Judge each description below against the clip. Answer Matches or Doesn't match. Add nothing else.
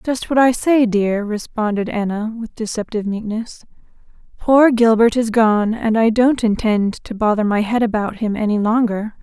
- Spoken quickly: Doesn't match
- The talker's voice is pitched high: Matches